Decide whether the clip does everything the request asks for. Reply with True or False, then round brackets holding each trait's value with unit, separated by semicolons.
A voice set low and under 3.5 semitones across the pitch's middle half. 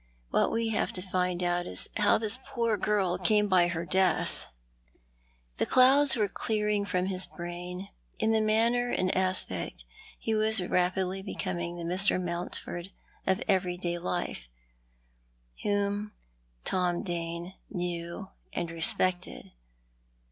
False (185 Hz; 3.1 semitones)